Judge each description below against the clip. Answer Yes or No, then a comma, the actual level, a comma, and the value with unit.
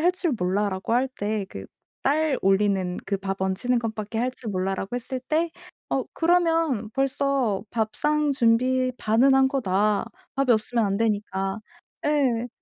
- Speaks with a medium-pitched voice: No, high, 230 Hz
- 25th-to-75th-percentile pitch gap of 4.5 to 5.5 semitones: Yes, average, 5.1 semitones